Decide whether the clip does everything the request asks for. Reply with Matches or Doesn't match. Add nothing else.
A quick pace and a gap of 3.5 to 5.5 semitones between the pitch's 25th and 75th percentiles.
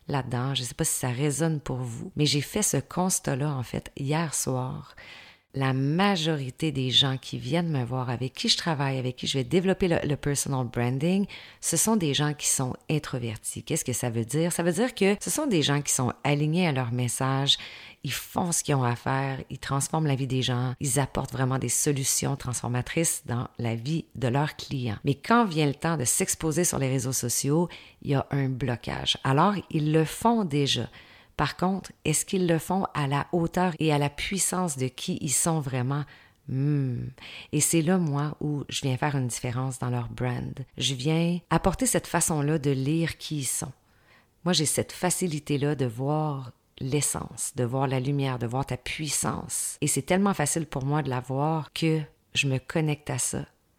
Doesn't match